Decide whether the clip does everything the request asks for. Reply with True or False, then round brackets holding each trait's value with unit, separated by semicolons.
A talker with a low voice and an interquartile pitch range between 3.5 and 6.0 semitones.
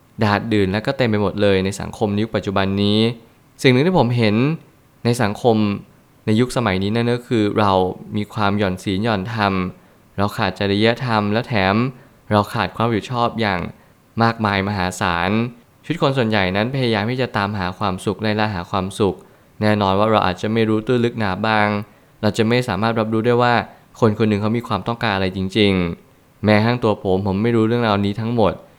False (110 Hz; 2.7 semitones)